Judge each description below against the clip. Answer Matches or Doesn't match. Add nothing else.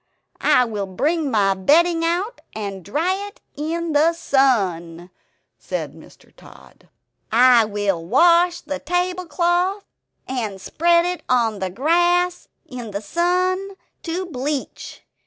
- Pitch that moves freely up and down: Matches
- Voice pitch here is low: Doesn't match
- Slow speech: Matches